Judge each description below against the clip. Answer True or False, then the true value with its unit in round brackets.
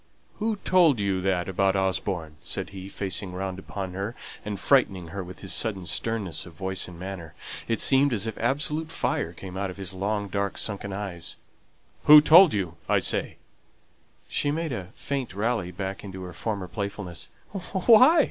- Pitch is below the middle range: True (100 Hz)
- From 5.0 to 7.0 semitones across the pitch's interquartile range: False (3.7 semitones)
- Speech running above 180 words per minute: False (175 wpm)